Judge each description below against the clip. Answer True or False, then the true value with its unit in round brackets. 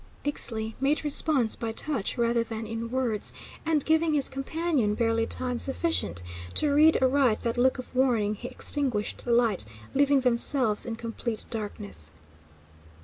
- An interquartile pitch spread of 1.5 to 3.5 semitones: False (3.9 semitones)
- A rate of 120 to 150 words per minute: True (145 wpm)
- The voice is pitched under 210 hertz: False (245 Hz)